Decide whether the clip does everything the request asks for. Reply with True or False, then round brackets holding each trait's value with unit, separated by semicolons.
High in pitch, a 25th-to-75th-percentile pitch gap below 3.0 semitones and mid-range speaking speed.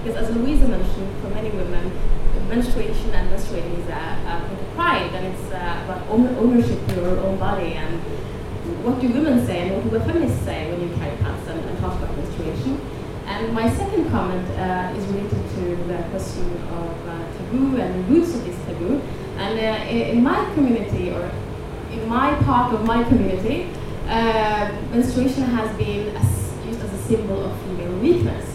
True (245 Hz; 2.4 semitones; 180 wpm)